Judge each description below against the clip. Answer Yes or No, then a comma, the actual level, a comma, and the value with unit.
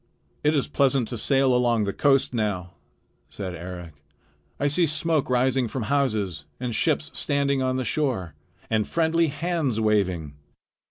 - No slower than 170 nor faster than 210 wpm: No, average, 150 wpm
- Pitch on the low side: Yes, low, 130 Hz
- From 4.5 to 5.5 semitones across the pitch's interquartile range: Yes, average, 5.2 semitones